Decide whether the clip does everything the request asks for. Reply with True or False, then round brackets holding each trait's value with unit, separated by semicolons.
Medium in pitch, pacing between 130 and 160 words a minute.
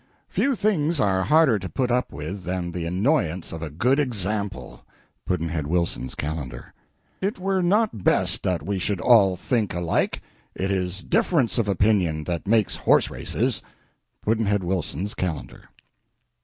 False (95 Hz; 145 wpm)